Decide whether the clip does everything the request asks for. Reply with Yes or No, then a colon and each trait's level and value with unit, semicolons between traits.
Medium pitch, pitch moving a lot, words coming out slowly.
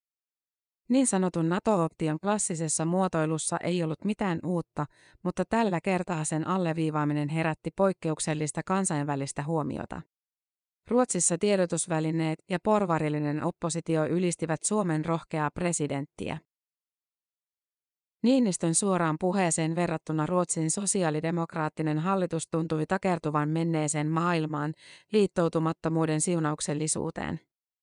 No: medium, 165 Hz; average, 2.8 semitones; slow, 85 wpm